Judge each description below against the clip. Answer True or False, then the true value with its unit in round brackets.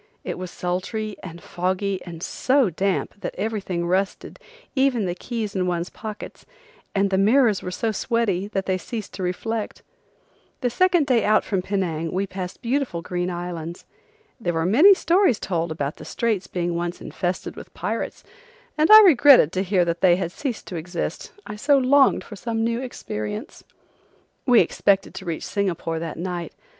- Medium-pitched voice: False (195 Hz)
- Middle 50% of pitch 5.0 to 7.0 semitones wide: False (4.6 semitones)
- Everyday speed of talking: True (170 wpm)